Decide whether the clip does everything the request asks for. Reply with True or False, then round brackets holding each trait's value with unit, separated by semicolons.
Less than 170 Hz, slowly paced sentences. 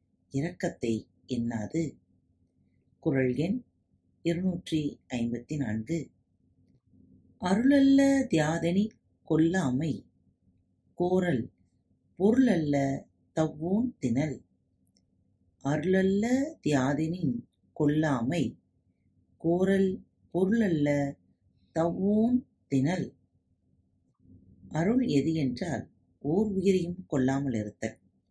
True (140 Hz; 60 wpm)